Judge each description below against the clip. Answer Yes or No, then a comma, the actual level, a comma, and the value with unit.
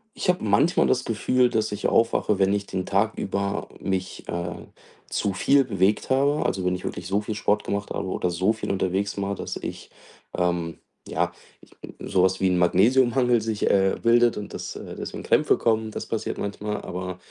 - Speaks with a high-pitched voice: No, low, 100 Hz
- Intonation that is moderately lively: Yes, average, 3.2 semitones